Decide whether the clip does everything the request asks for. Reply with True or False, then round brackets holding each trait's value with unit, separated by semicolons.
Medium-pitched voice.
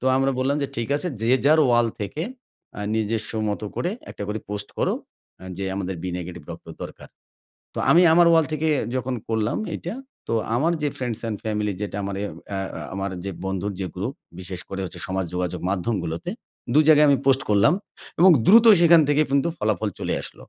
False (110 Hz)